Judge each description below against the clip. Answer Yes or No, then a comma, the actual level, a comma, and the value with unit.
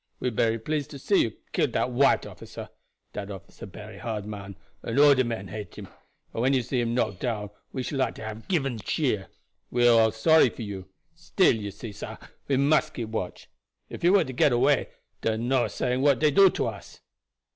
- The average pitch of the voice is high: No, low, 120 Hz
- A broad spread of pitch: No, average, 4.4 semitones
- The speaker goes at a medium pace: No, fast, 210 wpm